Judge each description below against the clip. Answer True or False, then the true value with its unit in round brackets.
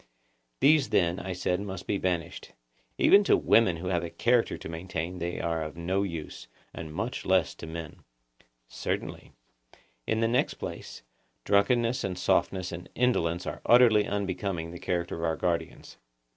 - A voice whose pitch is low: True (90 Hz)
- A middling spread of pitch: True (3.4 semitones)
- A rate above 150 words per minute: True (160 wpm)